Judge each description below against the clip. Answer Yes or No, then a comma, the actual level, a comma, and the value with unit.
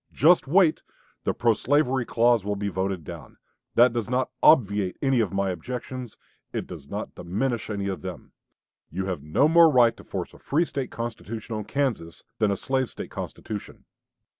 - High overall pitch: No, low, 115 Hz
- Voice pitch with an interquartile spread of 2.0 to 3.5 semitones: No, average, 4.9 semitones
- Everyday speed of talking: Yes, average, 180 wpm